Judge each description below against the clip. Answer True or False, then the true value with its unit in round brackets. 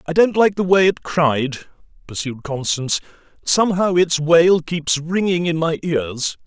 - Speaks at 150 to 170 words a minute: True (160 wpm)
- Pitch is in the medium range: True (165 Hz)